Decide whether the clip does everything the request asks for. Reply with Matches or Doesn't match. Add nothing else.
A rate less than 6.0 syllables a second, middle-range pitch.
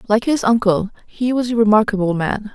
Doesn't match